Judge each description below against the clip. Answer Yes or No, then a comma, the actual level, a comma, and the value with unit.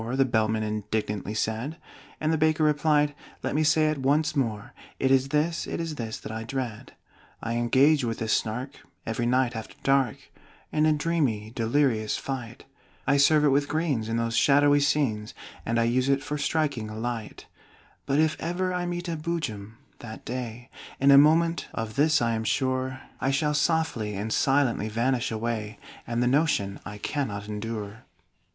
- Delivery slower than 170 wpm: No, average, 180 wpm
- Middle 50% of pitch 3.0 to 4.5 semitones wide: No, average, 4.9 semitones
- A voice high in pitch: No, low, 130 Hz